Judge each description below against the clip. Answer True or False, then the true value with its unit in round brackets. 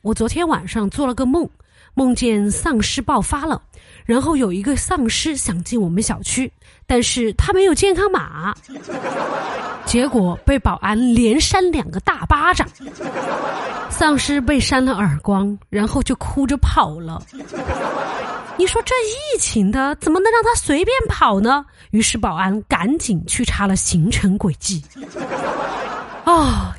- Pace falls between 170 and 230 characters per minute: True (210 characters per minute)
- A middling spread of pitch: False (7.4 semitones)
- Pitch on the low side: False (250 Hz)